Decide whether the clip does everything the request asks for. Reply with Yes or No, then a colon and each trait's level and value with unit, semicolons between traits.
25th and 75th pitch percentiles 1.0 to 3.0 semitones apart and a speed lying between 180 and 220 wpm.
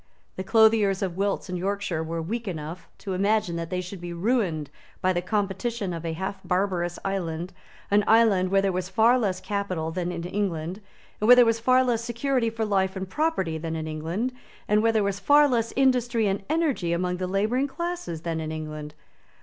No: average, 4.5 semitones; average, 200 wpm